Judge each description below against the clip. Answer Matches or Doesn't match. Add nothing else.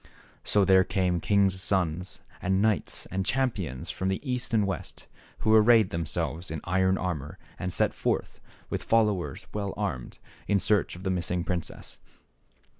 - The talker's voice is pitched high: Doesn't match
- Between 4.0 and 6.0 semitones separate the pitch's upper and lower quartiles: Doesn't match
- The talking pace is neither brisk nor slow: Matches